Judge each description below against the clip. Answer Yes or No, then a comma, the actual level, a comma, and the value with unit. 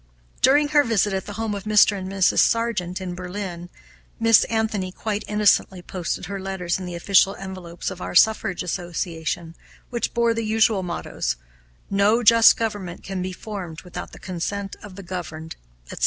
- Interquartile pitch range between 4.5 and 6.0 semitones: No, average, 3.2 semitones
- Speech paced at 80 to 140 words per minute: No, average, 170 wpm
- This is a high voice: Yes, high, 195 Hz